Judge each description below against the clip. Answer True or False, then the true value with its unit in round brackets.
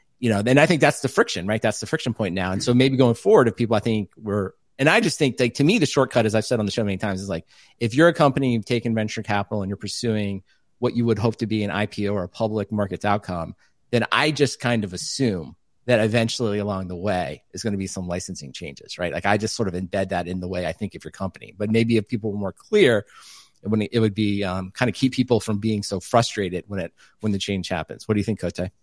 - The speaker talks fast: True (275 wpm)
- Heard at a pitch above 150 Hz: False (110 Hz)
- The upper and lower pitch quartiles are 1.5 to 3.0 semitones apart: False (3.4 semitones)